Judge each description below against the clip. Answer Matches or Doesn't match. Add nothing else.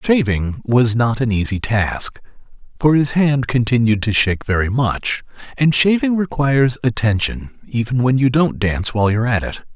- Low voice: Matches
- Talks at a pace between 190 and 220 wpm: Doesn't match